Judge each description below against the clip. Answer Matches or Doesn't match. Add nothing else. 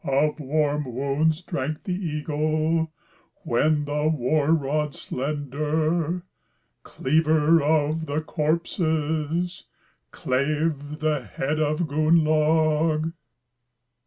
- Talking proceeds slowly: Matches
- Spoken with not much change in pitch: Matches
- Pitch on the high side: Doesn't match